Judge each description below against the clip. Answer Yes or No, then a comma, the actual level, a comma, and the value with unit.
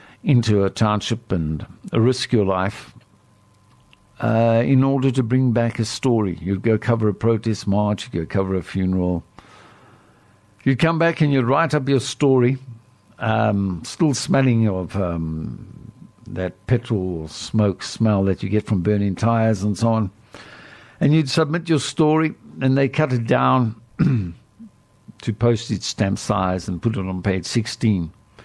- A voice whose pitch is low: Yes, low, 110 Hz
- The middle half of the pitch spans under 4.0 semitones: No, average, 4.5 semitones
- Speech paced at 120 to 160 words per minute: Yes, average, 155 wpm